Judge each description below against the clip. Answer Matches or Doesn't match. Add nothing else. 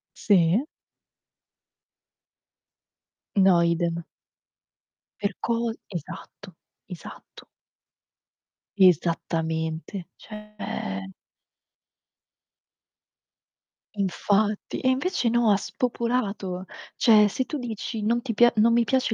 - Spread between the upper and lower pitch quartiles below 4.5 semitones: Doesn't match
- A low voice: Doesn't match